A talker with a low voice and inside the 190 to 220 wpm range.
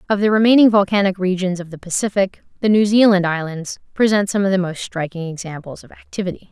No: high, 190 Hz; average, 195 wpm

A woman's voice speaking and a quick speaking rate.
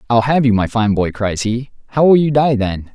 No: male; fast, 265 wpm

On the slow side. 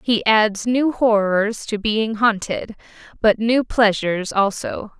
Yes: slow, 130 wpm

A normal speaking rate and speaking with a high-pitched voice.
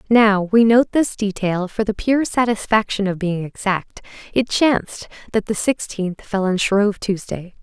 Yes: average, 165 wpm; high, 210 Hz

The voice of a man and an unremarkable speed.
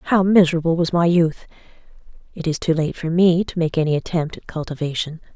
No: female; average, 190 wpm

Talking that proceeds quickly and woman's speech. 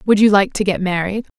Yes: fast, 260 wpm; female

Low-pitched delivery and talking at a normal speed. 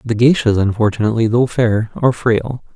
Yes: low, 115 Hz; average, 155 wpm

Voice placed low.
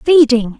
No: very high, 265 Hz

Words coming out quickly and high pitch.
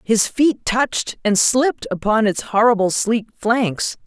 No: average, 150 wpm; high, 225 Hz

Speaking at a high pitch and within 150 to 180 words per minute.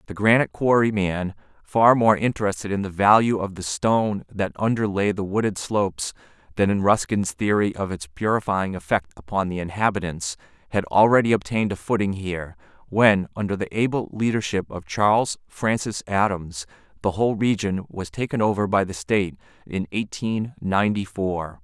No: low, 100 Hz; average, 155 wpm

